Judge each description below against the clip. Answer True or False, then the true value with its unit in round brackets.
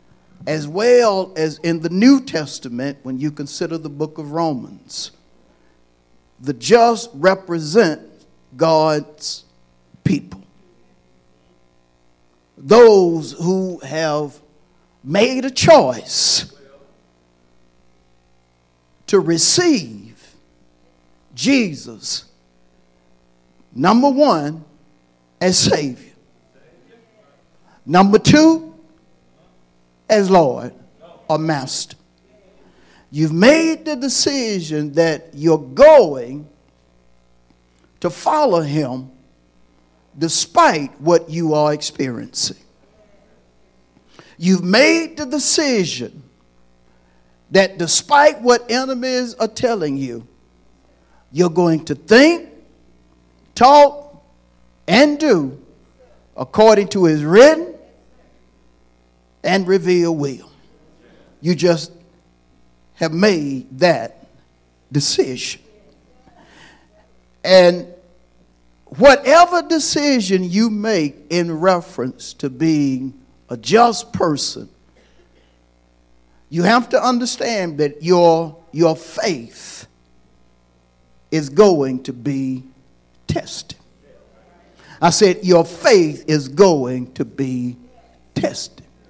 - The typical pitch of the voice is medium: True (150 Hz)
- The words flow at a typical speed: False (80 wpm)